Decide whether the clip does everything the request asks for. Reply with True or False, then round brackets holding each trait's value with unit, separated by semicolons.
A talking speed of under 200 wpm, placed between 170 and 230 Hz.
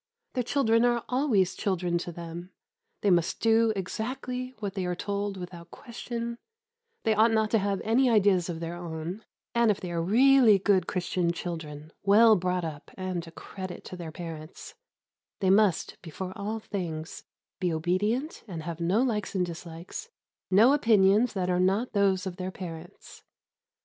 True (165 wpm; 190 Hz)